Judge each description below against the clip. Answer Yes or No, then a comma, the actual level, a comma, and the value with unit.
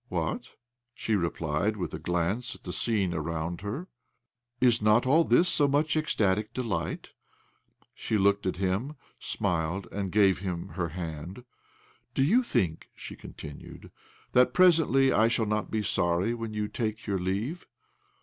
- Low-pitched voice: Yes, low, 105 Hz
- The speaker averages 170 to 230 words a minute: Yes, average, 180 wpm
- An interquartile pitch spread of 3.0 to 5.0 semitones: No, wide, 5.5 semitones